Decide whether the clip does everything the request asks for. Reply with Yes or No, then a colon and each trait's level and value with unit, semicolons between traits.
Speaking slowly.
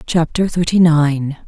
Yes: slow, 120 wpm